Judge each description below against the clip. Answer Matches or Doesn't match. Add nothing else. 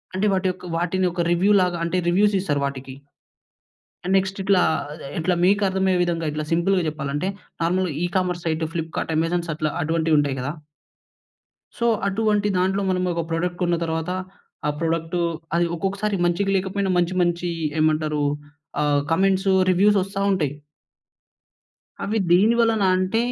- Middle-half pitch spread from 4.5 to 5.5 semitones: Doesn't match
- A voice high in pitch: Doesn't match